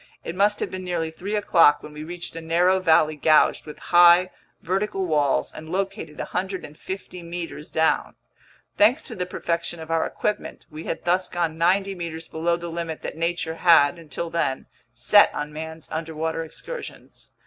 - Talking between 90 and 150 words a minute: No, average, 170 wpm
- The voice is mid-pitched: Yes, medium, 170 Hz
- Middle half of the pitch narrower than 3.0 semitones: Yes, narrow, 2.4 semitones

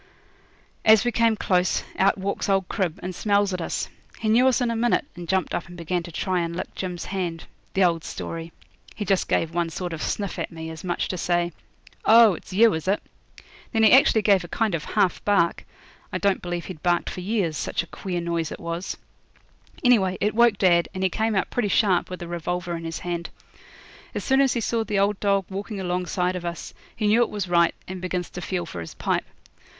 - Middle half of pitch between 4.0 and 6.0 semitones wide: No, average, 3.1 semitones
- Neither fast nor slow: No, fast, 230 wpm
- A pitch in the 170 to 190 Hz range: Yes, medium, 185 Hz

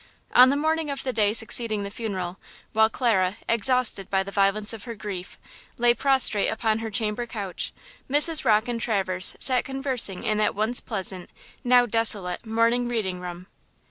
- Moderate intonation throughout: Yes, average, 3.5 semitones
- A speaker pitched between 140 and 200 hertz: No, high, 220 Hz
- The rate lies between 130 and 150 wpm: No, average, 170 wpm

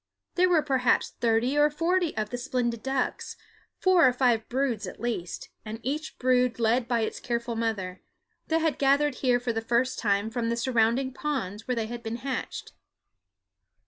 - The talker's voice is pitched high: Yes, high, 245 Hz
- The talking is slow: No, average, 175 wpm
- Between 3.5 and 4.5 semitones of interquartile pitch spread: No, average, 3.1 semitones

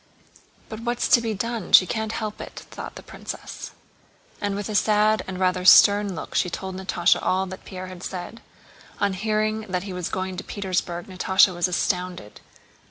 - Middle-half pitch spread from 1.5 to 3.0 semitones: Yes, narrow, 2.6 semitones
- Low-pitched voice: No, high, 190 Hz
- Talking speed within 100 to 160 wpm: No, average, 180 wpm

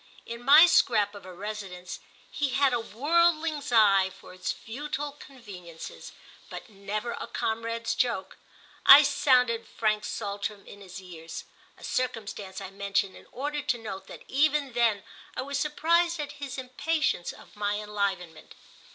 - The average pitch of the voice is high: Yes, high, 230 Hz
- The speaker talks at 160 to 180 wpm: No, average, 145 wpm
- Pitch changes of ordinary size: No, wide, 6.0 semitones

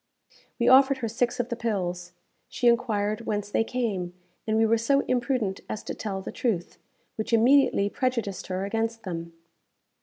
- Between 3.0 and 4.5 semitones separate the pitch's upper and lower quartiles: Yes, average, 3.5 semitones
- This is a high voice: Yes, high, 225 Hz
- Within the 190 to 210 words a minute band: No, average, 170 wpm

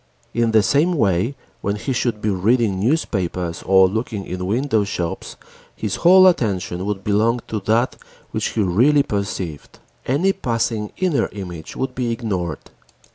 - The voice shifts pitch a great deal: No, average, 4.6 semitones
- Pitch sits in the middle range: No, low, 105 Hz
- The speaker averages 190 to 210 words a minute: No, average, 145 wpm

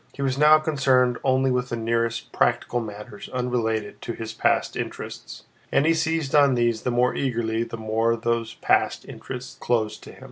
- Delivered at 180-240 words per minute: Yes, average, 185 wpm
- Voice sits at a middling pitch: No, low, 120 Hz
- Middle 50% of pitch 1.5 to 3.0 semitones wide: Yes, narrow, 2.6 semitones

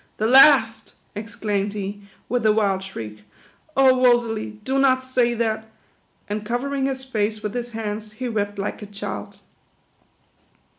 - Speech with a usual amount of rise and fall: Yes, average, 3.4 semitones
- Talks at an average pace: Yes, average, 155 wpm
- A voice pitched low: No, high, 220 Hz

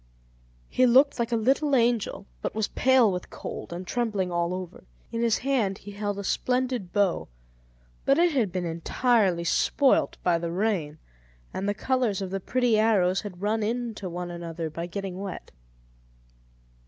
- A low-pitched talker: No, high, 205 Hz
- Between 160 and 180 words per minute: Yes, average, 165 wpm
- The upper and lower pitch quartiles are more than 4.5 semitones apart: Yes, average, 5.0 semitones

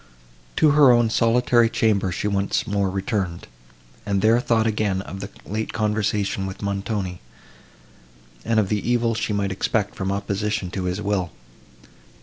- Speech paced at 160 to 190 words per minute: No, average, 150 wpm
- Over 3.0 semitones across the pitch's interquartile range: No, narrow, 2.4 semitones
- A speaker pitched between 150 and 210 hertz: No, low, 105 Hz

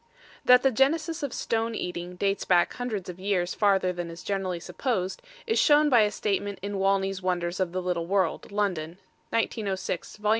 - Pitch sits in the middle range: No, high, 195 Hz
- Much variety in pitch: No, average, 3.7 semitones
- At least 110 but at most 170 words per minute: No, average, 180 wpm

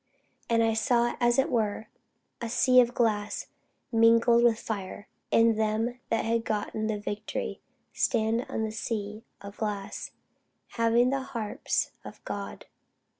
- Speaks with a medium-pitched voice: No, high, 225 Hz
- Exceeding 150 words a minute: No, average, 140 wpm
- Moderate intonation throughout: No, narrow, 1.7 semitones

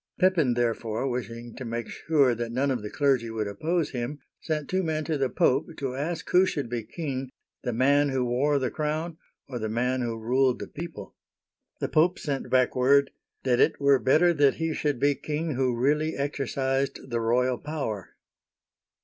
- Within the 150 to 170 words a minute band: No, average, 190 wpm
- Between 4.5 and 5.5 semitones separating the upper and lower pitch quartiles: No, average, 3.7 semitones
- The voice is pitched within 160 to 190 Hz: No, low, 135 Hz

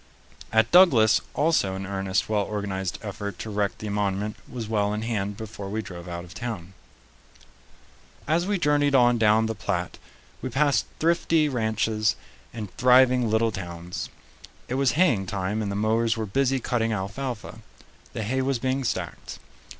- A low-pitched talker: Yes, low, 110 Hz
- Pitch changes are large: No, average, 4.2 semitones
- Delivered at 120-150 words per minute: No, average, 160 wpm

